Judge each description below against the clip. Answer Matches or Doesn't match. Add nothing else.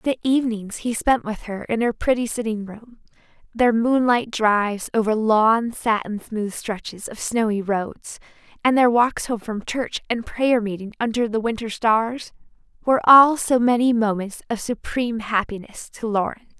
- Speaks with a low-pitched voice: Doesn't match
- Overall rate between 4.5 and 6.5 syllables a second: Matches